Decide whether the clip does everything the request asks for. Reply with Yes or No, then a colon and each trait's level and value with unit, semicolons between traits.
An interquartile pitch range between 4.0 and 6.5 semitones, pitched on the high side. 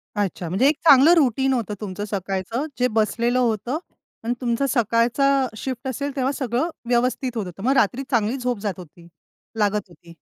Yes: average, 4.3 semitones; high, 235 Hz